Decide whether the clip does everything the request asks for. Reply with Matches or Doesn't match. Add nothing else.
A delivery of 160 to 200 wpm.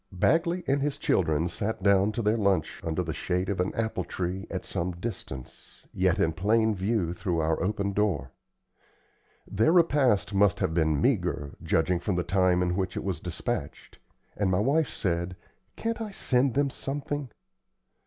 Matches